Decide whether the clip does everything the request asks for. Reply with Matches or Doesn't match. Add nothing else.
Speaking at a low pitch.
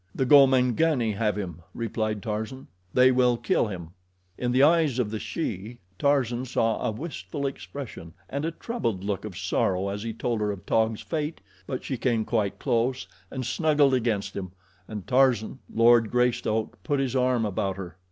Matches